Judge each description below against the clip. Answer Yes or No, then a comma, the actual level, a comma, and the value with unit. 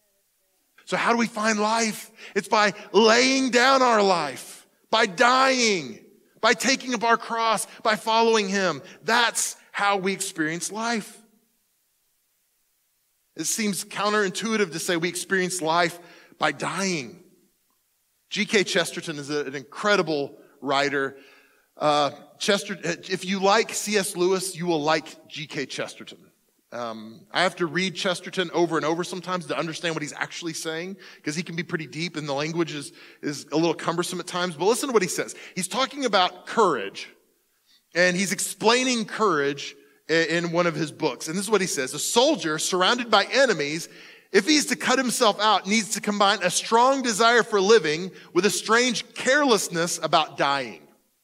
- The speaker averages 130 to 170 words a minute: Yes, average, 160 wpm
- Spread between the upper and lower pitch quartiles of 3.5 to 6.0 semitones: Yes, average, 5.1 semitones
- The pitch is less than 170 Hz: No, high, 190 Hz